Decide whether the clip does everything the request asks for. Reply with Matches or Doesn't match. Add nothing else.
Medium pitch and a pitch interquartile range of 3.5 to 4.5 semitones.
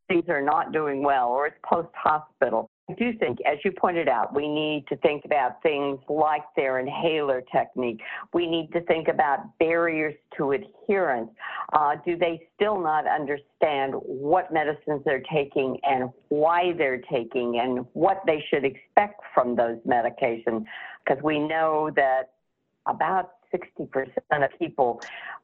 Matches